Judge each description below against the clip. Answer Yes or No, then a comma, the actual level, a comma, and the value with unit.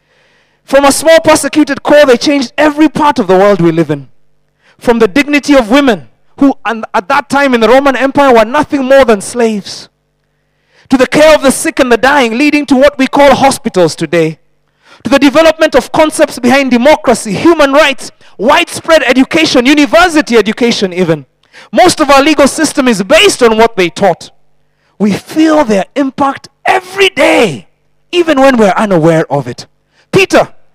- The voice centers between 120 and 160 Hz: No, very high, 270 Hz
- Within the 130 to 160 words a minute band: No, average, 170 wpm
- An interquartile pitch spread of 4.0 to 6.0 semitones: Yes, average, 5.2 semitones